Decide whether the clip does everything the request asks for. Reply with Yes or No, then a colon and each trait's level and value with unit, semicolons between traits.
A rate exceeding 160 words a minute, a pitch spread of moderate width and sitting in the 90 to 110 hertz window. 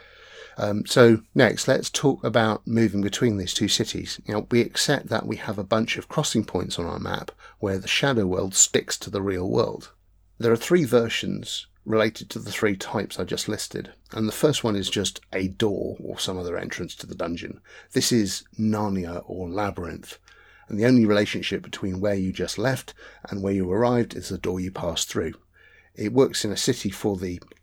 Yes: average, 200 wpm; average, 3.3 semitones; low, 105 Hz